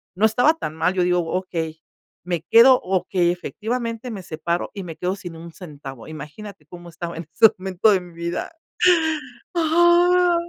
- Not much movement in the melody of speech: No, average, 4.9 semitones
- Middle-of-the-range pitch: Yes, medium, 180 Hz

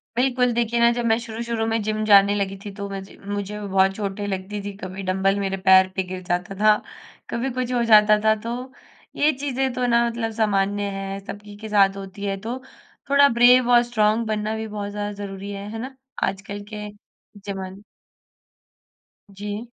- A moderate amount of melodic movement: Yes, average, 3.1 semitones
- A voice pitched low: No, high, 210 Hz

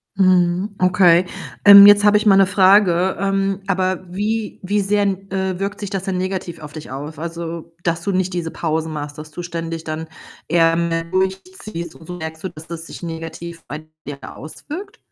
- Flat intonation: No, average, 3.0 semitones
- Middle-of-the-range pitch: Yes, medium, 180 Hz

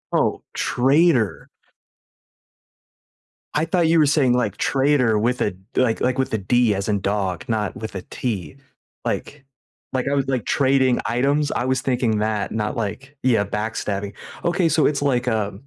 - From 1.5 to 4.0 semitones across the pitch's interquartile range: No, average, 4.6 semitones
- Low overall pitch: Yes, low, 125 Hz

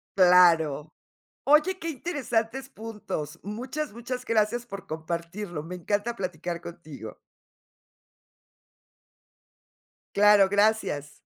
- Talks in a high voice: Yes, high, 205 Hz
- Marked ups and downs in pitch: Yes, wide, 5.7 semitones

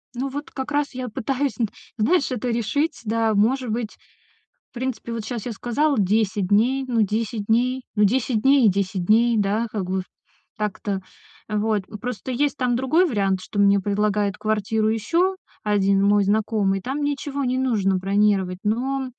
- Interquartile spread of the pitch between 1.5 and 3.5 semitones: No, average, 4.0 semitones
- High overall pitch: Yes, high, 220 Hz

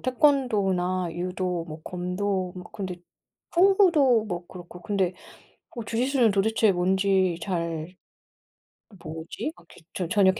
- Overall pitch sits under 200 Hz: Yes, high, 190 Hz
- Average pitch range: Yes, average, 3.8 semitones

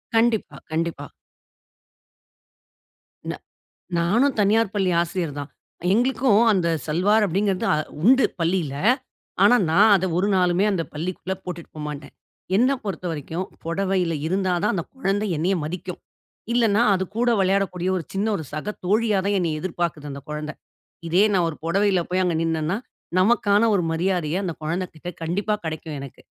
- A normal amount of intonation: Yes, average, 3.7 semitones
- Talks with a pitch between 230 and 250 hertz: No, medium, 185 Hz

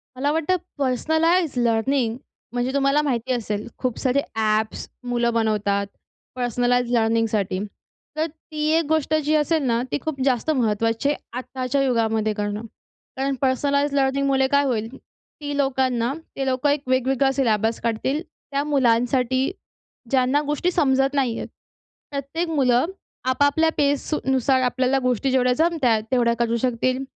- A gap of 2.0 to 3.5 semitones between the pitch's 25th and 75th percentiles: Yes, average, 3.2 semitones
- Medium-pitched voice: No, very high, 260 Hz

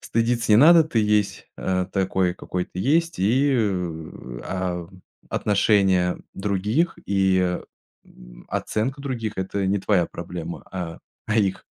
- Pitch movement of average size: Yes, average, 3.7 semitones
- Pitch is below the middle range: Yes, very low, 95 Hz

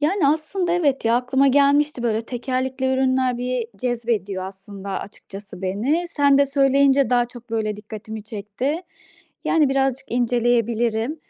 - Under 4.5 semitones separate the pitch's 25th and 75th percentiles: Yes, average, 3.9 semitones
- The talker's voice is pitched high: Yes, very high, 250 Hz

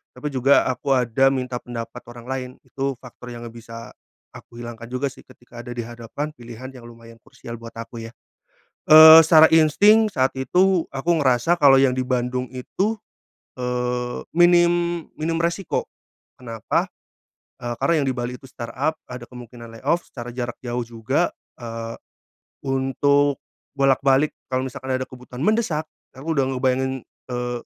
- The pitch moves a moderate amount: Yes, average, 3.2 semitones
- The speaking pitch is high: No, low, 130 Hz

